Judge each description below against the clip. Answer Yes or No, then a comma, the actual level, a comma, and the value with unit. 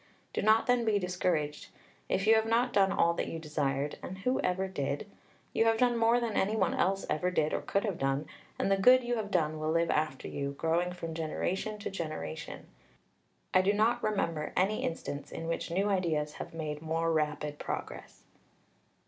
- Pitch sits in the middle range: Yes, medium, 180 Hz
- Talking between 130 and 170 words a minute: No, average, 195 wpm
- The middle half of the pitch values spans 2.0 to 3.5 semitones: No, average, 5.2 semitones